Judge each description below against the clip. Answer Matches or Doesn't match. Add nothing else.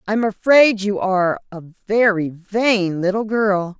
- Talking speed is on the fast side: Doesn't match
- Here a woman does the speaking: Matches